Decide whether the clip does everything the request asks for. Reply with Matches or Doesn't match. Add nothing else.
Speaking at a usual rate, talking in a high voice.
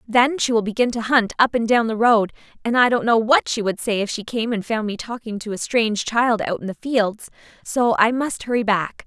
Doesn't match